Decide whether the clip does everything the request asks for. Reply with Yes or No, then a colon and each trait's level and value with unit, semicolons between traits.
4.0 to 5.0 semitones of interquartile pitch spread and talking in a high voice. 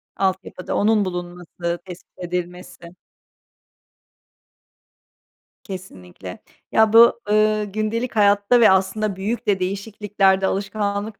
No: average, 2.7 semitones; high, 195 Hz